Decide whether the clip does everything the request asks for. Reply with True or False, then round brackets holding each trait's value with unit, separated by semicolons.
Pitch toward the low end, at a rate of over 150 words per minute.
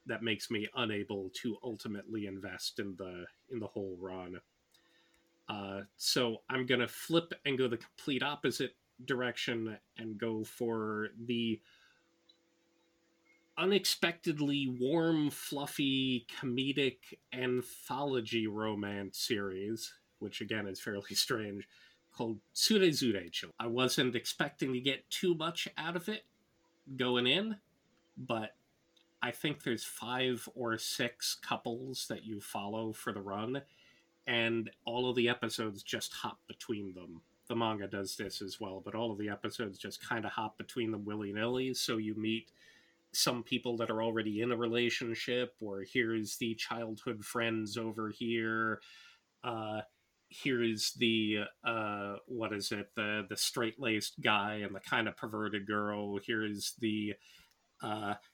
False (115 Hz; 135 wpm)